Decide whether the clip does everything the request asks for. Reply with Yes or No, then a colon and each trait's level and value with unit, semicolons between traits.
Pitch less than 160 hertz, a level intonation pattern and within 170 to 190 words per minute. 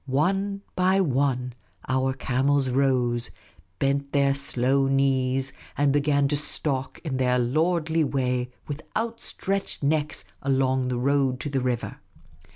No: low, 135 Hz; narrow, 2.2 semitones; slow, 135 wpm